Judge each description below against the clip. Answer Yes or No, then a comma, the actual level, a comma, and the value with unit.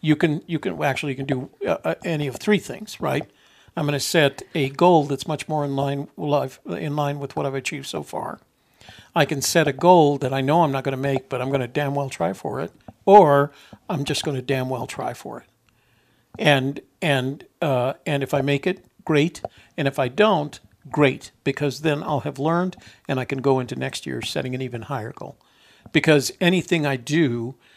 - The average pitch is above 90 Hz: Yes, medium, 140 Hz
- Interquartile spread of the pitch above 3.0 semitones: No, narrow, 2.5 semitones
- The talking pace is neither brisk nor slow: No, fast, 215 wpm